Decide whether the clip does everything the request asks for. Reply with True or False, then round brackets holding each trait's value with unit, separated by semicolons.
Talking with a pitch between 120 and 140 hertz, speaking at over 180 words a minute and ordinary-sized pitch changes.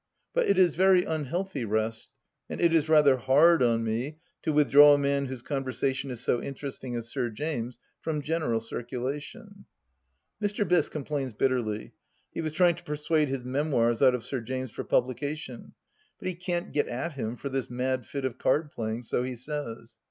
True (135 Hz; 190 wpm; 4.1 semitones)